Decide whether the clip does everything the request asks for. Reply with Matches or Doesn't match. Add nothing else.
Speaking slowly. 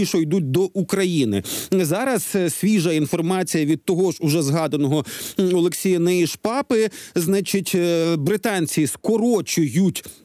Matches